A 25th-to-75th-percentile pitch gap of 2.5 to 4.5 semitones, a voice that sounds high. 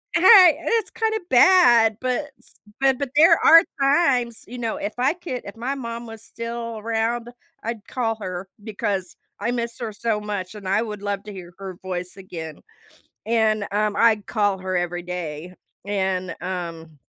Yes: average, 4.1 semitones; high, 220 Hz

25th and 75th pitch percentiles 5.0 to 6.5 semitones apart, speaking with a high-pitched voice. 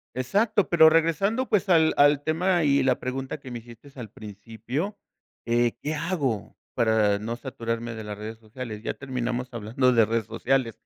No: wide, 5.4 semitones; low, 125 Hz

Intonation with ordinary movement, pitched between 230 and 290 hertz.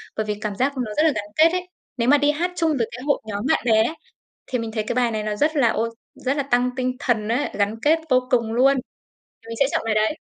Yes: average, 4.5 semitones; very high, 250 Hz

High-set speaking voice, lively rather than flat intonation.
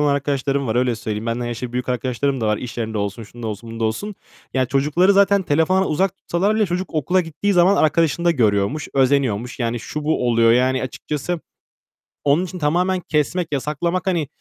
No: medium, 140 Hz; wide, 6.3 semitones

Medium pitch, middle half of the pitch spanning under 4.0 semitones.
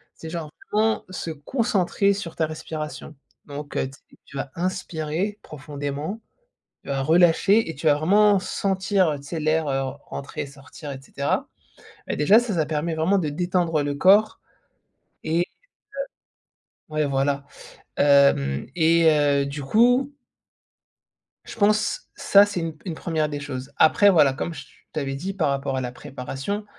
No: medium, 155 Hz; average, 4.9 semitones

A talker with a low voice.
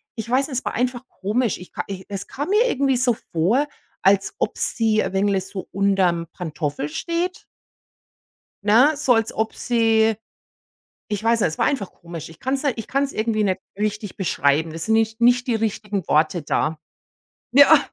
No: high, 215 Hz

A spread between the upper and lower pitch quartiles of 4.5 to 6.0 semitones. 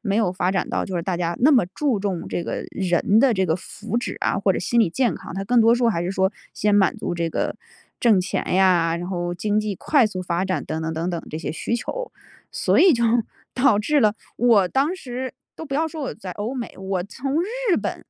Yes: wide, 5.4 semitones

